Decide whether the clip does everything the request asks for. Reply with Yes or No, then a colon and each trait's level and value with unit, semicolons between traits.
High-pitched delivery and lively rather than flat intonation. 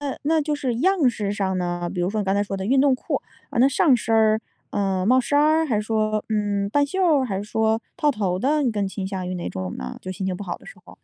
Yes: high, 215 Hz; wide, 6.0 semitones